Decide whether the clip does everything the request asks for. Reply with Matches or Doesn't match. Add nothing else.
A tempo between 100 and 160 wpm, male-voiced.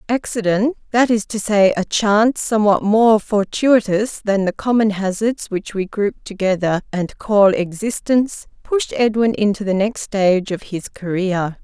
Doesn't match